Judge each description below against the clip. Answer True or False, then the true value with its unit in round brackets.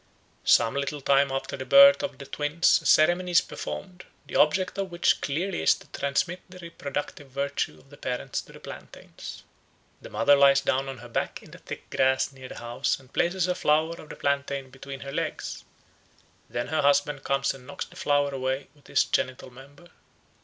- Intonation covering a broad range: False (3.8 semitones)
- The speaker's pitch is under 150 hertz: True (140 Hz)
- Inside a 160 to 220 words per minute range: True (195 wpm)